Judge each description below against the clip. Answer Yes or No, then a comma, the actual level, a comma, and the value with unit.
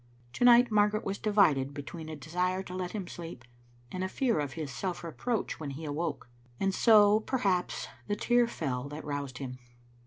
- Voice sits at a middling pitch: Yes, medium, 180 Hz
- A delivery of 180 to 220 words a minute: Yes, average, 185 wpm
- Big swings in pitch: Yes, wide, 6.0 semitones